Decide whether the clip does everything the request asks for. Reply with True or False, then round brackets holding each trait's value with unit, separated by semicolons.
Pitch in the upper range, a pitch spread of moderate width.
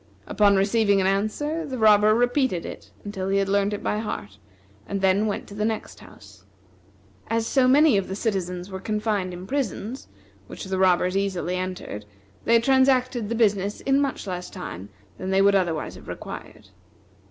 True (200 Hz; 3.5 semitones)